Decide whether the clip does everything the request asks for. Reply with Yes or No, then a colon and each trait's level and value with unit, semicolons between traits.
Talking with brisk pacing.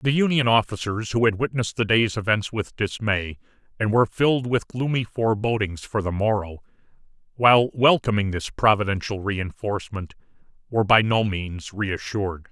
No: average, 145 wpm